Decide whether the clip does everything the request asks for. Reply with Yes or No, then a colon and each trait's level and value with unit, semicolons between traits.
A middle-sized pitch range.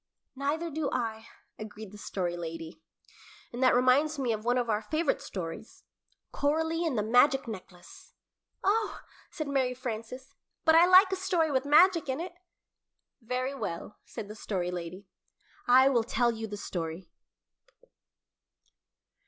No: wide, 6.6 semitones